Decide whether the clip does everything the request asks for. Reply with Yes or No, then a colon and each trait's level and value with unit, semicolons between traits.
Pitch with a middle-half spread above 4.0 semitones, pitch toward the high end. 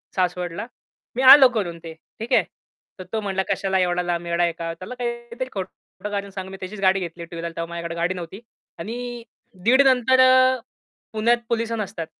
Yes: wide, 5.5 semitones; high, 195 Hz